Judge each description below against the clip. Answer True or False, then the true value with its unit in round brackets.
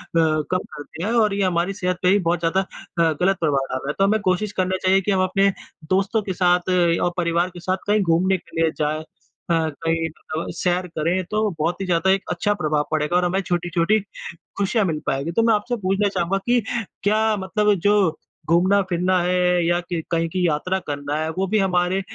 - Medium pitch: True (180 Hz)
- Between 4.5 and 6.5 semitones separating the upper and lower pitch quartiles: False (2.8 semitones)